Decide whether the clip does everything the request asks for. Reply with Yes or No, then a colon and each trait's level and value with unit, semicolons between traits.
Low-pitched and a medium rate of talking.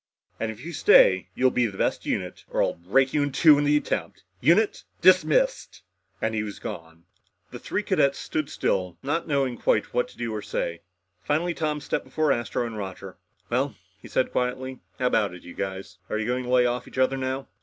No: low, 125 Hz; fast, 215 wpm